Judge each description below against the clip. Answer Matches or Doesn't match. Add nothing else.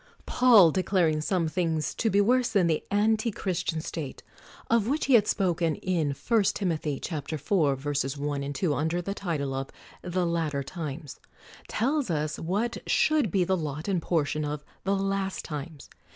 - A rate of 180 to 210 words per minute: Doesn't match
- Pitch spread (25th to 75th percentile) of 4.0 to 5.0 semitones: Matches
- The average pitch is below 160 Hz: Doesn't match